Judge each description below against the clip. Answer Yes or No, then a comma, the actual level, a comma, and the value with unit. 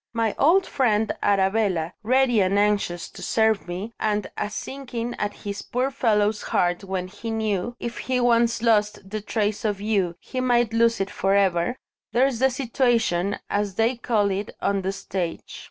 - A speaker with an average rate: Yes, average, 170 wpm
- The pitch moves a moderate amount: Yes, average, 3.1 semitones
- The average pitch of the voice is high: Yes, high, 215 Hz